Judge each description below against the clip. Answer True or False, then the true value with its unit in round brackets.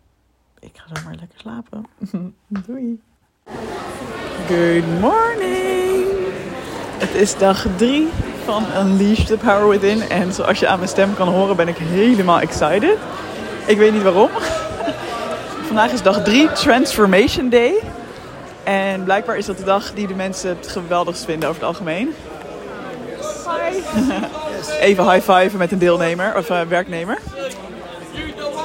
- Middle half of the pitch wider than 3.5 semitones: True (4.4 semitones)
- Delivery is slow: True (130 wpm)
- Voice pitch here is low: False (200 Hz)